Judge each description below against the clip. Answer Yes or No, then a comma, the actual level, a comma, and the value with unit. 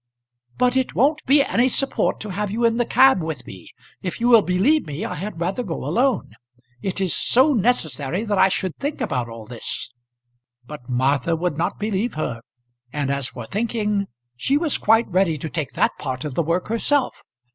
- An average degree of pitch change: No, wide, 8.0 semitones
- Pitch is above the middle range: Yes, high, 195 Hz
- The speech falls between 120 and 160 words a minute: No, average, 195 wpm